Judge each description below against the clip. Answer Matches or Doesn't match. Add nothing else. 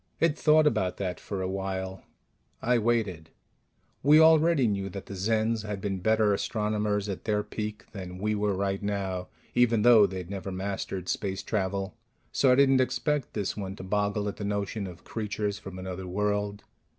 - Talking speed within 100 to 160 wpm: Doesn't match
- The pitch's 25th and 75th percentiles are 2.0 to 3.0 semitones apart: Matches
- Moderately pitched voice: Doesn't match